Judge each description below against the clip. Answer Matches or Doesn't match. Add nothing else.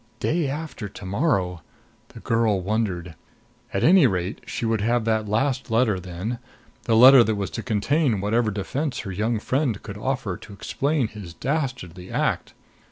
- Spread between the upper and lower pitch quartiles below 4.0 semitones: Doesn't match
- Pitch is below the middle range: Matches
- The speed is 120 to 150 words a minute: Doesn't match